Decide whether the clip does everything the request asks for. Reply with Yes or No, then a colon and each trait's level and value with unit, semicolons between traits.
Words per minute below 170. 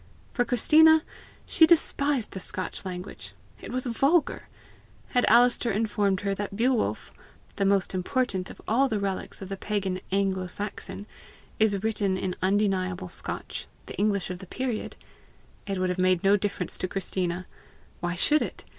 Yes: average, 155 wpm